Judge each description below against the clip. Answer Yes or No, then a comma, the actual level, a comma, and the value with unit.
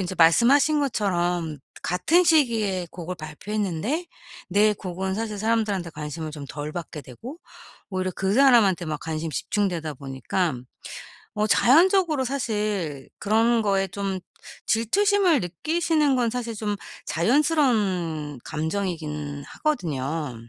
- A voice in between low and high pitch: No, high, 195 Hz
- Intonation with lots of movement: Yes, wide, 6.7 semitones